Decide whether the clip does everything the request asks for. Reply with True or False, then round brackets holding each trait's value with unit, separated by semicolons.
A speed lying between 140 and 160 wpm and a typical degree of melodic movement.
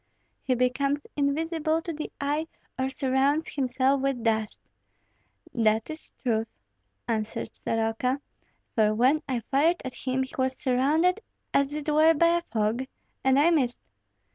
True (145 wpm; 4.0 semitones)